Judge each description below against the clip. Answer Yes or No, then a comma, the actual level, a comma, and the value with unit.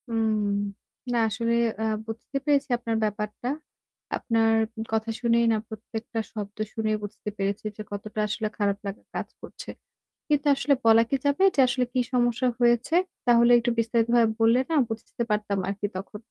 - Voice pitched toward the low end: No, high, 225 Hz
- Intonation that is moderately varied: No, narrow, 2.1 semitones